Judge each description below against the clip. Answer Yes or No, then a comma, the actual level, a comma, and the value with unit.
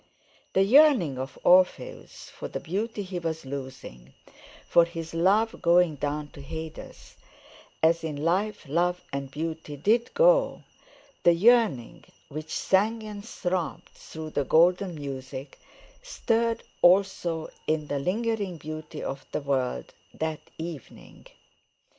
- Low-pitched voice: No, medium, 165 Hz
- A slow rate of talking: Yes, slow, 125 wpm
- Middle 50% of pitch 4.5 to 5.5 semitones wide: Yes, average, 5.2 semitones